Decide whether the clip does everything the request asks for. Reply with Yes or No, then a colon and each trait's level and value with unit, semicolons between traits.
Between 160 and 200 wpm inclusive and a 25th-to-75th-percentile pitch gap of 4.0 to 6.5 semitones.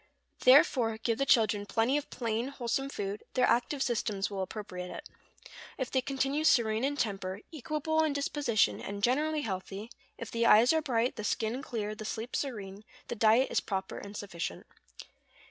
Yes: average, 170 wpm; average, 4.6 semitones